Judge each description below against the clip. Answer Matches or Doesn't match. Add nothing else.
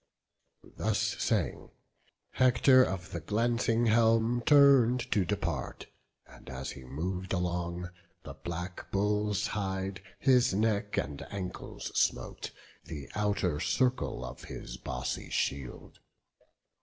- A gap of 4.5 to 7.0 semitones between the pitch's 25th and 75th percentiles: Matches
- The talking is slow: Matches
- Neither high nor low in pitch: Doesn't match